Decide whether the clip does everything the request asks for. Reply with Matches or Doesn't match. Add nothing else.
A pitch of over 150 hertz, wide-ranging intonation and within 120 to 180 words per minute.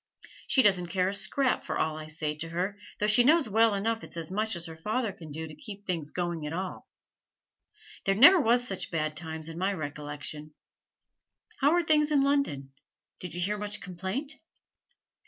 Doesn't match